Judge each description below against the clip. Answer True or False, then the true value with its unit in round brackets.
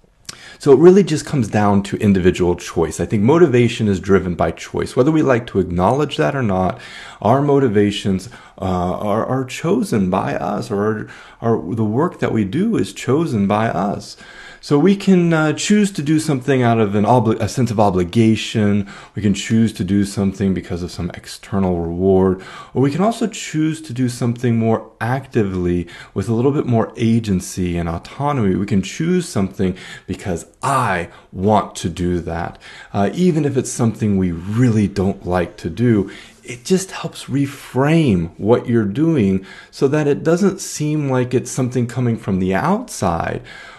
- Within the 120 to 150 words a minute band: False (175 wpm)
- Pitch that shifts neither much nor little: False (6.2 semitones)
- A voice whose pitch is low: True (115 Hz)